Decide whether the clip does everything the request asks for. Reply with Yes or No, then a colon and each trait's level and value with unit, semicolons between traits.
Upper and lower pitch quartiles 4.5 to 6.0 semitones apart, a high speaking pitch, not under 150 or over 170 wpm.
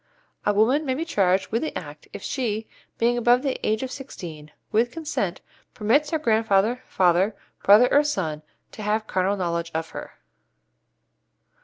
Yes: average, 5.2 semitones; high, 220 Hz; average, 160 wpm